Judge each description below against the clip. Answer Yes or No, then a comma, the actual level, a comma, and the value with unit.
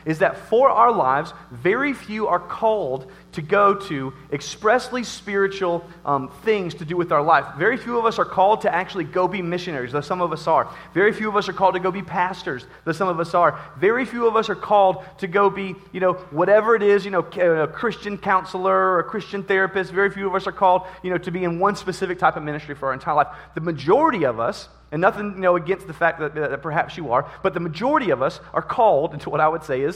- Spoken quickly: Yes, fast, 250 wpm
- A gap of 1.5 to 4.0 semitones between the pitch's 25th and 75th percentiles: Yes, average, 3.0 semitones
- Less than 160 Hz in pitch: No, medium, 185 Hz